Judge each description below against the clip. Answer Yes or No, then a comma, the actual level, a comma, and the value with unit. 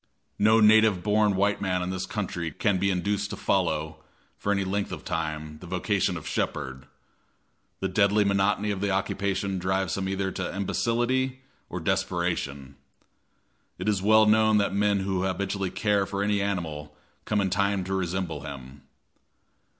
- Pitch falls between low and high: No, very low, 95 Hz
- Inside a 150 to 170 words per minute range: Yes, average, 160 wpm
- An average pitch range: No, narrow, 2.3 semitones